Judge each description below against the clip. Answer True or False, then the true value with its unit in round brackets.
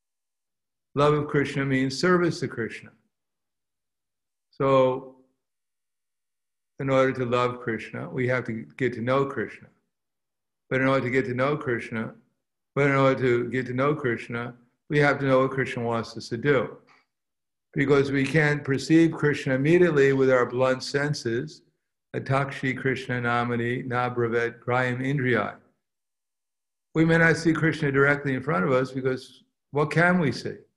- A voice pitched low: True (130 Hz)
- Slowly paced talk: False (150 wpm)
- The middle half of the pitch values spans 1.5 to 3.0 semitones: True (2.5 semitones)